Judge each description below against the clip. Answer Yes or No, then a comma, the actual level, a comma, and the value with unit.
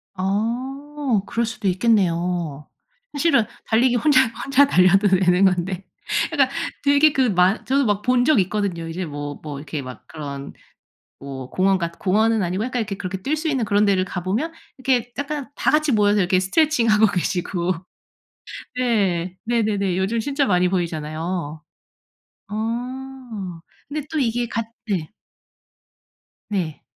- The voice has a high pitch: Yes, high, 205 Hz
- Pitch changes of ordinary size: No, wide, 5.9 semitones